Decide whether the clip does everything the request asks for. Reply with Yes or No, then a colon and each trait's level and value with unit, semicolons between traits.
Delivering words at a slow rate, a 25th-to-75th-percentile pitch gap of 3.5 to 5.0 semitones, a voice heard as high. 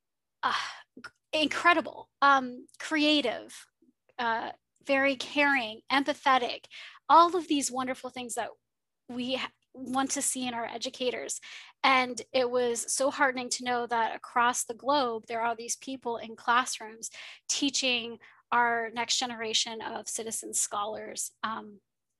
No: slow, 125 wpm; average, 3.0 semitones; very high, 250 Hz